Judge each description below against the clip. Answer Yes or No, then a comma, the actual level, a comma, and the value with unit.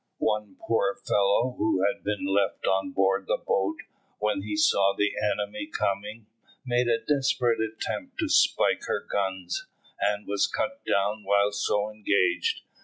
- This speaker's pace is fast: No, average, 150 wpm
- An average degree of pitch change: No, narrow, 2.0 semitones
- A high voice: No, low, 105 Hz